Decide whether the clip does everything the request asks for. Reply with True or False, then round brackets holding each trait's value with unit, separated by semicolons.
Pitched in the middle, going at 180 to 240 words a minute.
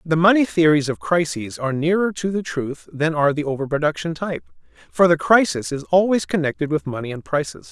True (155 Hz; 200 wpm)